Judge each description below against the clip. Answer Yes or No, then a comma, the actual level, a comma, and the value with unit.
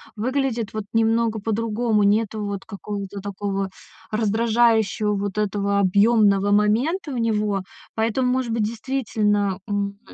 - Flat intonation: Yes, narrow, 2.2 semitones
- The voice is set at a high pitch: Yes, high, 215 Hz